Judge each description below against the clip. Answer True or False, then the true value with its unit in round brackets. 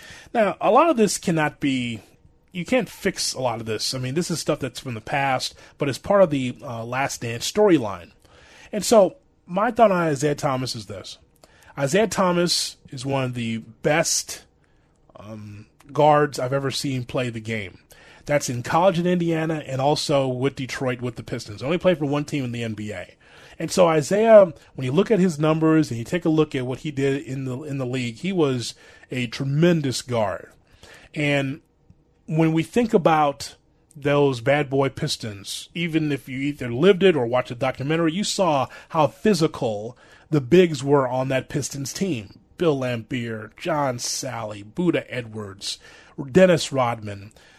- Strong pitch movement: False (4.7 semitones)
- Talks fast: False (180 wpm)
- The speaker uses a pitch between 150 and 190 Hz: False (140 Hz)